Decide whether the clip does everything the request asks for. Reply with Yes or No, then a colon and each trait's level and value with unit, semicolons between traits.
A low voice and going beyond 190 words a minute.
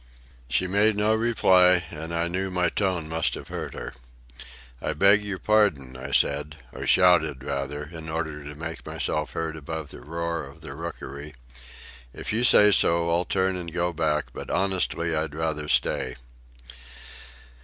No: very low, 85 Hz; average, 165 wpm